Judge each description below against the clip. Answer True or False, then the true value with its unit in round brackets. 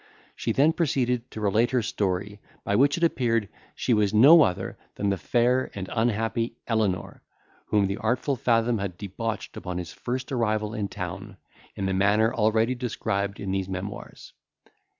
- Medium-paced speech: True (165 wpm)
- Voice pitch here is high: False (110 Hz)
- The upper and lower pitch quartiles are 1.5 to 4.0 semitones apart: True (3.5 semitones)